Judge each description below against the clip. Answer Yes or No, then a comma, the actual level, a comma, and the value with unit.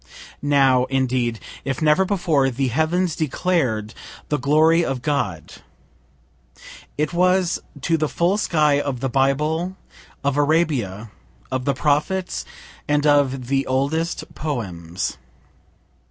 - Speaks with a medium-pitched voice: Yes, medium, 145 Hz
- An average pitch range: Yes, average, 3.7 semitones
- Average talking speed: No, slow, 115 wpm